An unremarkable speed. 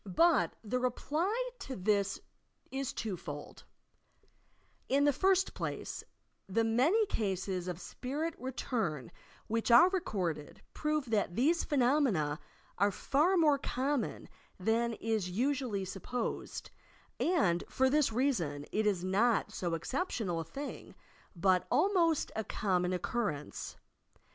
No: slow, 125 wpm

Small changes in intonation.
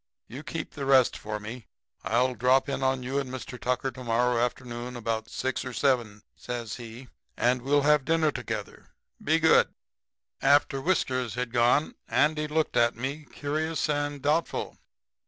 No: average, 3.3 semitones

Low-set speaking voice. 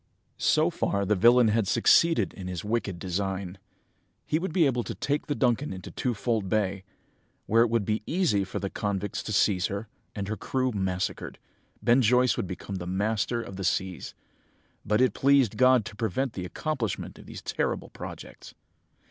Yes: low, 105 Hz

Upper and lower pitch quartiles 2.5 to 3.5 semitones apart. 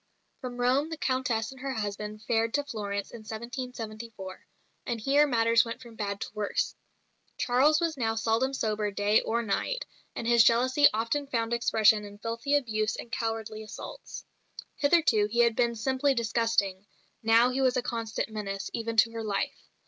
Yes: average, 2.8 semitones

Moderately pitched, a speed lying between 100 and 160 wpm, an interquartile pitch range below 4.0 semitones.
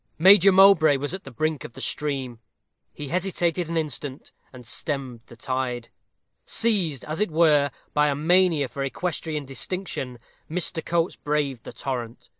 No: medium, 150 Hz; average, 155 wpm; average, 4.4 semitones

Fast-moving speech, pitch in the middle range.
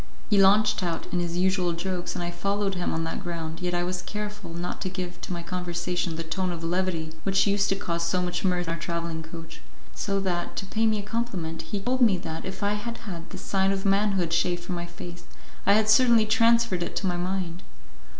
Yes: fast, 230 wpm; medium, 180 Hz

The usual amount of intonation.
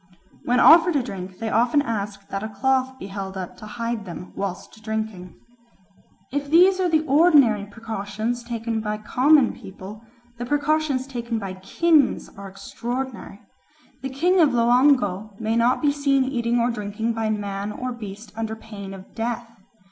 Yes: average, 4.4 semitones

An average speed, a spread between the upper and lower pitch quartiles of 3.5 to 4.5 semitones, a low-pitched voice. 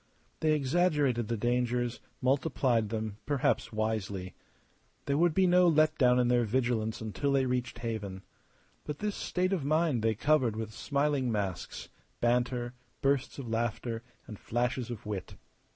Yes: average, 150 wpm; average, 4.2 semitones; low, 125 Hz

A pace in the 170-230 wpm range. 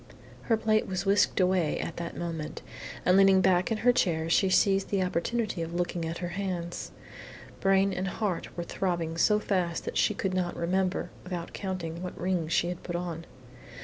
Yes: average, 185 wpm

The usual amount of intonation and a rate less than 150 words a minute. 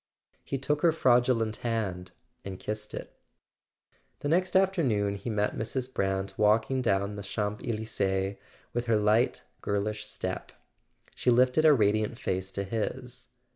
Yes: average, 3.8 semitones; average, 140 wpm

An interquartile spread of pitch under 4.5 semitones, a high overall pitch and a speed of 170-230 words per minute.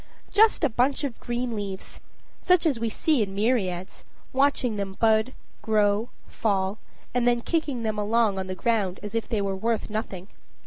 Yes: average, 3.5 semitones; high, 220 Hz; average, 175 wpm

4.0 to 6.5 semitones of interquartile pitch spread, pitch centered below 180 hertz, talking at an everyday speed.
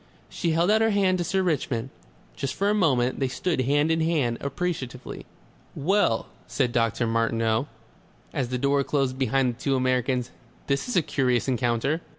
Yes: average, 4.7 semitones; low, 135 Hz; average, 170 wpm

